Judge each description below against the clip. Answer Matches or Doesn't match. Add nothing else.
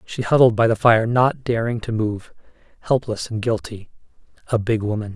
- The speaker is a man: Matches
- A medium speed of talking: Matches